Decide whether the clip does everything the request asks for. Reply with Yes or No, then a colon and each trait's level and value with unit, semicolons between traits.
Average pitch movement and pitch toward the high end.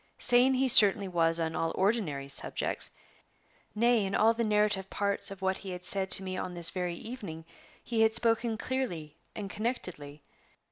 Yes: average, 4.5 semitones; high, 195 Hz